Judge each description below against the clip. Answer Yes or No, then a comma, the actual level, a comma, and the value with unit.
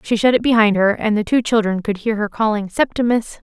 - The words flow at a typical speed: No, fast, 240 wpm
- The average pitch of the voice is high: Yes, high, 215 Hz